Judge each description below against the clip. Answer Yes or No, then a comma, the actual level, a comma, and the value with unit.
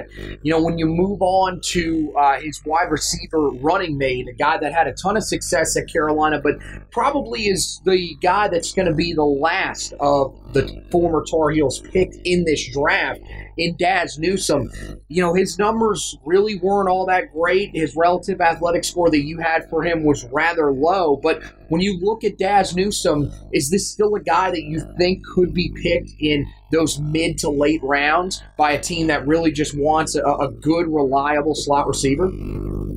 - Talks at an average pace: Yes, average, 190 wpm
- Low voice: No, medium, 160 Hz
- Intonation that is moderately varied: Yes, average, 3.5 semitones